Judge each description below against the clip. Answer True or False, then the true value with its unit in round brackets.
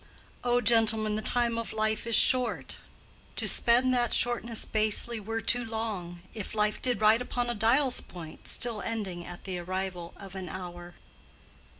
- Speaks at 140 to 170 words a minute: True (165 wpm)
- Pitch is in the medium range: False (220 Hz)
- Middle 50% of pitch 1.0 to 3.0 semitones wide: False (3.8 semitones)